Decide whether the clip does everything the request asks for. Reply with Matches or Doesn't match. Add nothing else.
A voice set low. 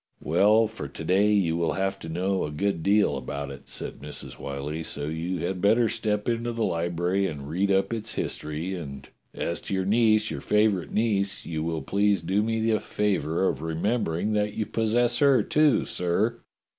Matches